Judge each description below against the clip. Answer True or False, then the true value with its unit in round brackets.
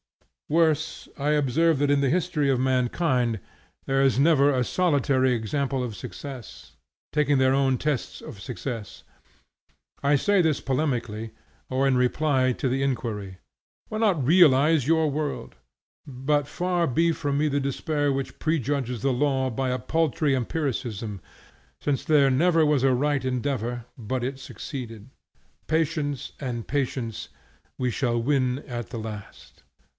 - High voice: False (135 Hz)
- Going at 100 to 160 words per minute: True (145 wpm)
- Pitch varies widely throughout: False (3.1 semitones)